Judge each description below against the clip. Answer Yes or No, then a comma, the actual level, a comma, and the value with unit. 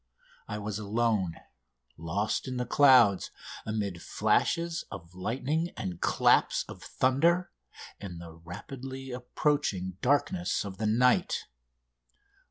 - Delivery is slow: Yes, slow, 110 wpm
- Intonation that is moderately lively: No, wide, 6.0 semitones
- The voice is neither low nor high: No, low, 110 Hz